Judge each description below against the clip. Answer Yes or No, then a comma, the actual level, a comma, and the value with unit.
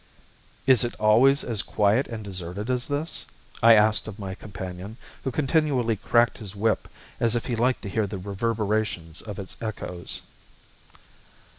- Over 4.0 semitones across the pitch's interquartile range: No, average, 3.1 semitones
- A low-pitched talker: Yes, low, 110 Hz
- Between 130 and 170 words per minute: Yes, average, 155 wpm